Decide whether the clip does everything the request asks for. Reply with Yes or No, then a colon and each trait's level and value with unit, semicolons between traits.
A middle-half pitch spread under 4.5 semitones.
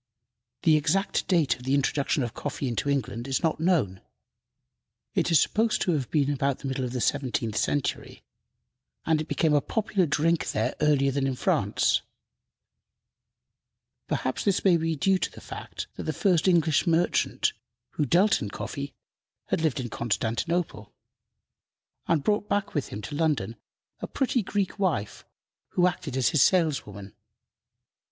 No: average, 5.0 semitones